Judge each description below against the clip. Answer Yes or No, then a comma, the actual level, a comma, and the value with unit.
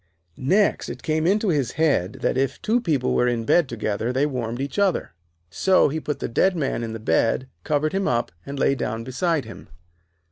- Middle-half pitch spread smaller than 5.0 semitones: No, wide, 5.4 semitones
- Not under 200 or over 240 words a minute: Yes, fast, 205 wpm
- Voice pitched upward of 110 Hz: Yes, medium, 140 Hz